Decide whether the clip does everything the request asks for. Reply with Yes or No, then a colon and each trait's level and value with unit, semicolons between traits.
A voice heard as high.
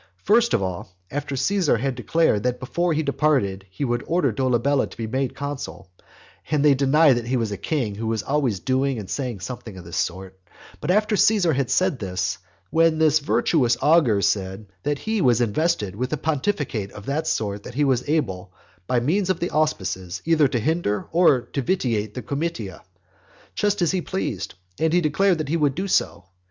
No: low, 135 Hz